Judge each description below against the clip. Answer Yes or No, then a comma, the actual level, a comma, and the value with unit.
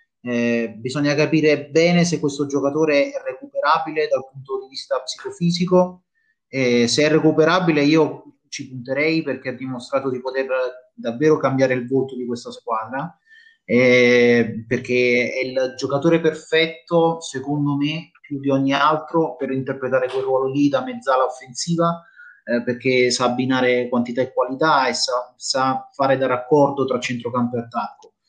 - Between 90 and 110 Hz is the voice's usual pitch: No, low, 135 Hz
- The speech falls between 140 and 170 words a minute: Yes, average, 150 wpm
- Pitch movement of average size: Yes, average, 3.8 semitones